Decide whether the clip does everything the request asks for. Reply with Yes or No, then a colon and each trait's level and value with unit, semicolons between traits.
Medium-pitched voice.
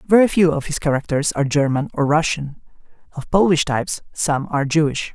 Yes: medium, 150 Hz